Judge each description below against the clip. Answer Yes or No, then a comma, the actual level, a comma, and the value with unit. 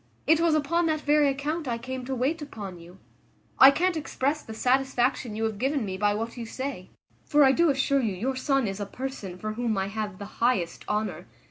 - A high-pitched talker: Yes, very high, 255 Hz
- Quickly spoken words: Yes, fast, 220 wpm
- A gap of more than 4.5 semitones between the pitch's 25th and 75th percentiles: Yes, average, 5.0 semitones